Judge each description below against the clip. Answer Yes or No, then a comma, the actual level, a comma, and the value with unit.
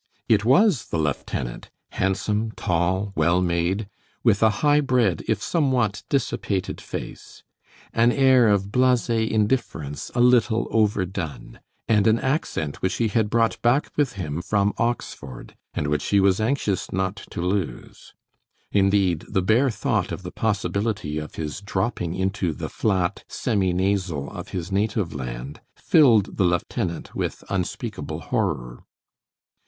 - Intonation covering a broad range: No, average, 4.3 semitones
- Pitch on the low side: Yes, low, 100 Hz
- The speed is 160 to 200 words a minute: No, average, 140 wpm